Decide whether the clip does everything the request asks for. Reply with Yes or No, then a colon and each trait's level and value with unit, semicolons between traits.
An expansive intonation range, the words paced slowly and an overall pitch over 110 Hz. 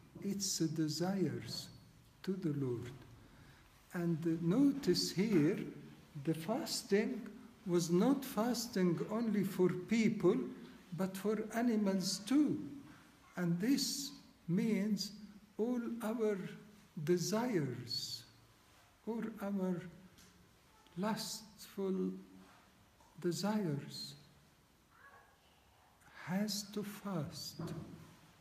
No: average, 4.8 semitones; slow, 70 wpm; high, 190 Hz